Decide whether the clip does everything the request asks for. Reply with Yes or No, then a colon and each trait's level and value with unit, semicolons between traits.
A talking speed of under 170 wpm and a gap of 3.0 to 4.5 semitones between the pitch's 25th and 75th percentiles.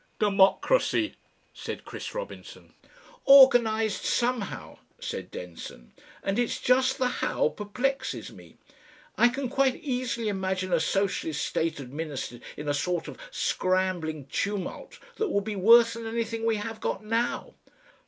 No: slow, 135 wpm; average, 5.0 semitones